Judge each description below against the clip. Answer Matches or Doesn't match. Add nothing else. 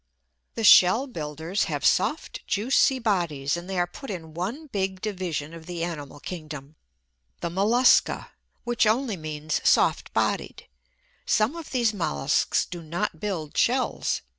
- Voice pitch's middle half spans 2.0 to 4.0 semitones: Doesn't match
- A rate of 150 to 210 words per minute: Doesn't match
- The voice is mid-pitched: Matches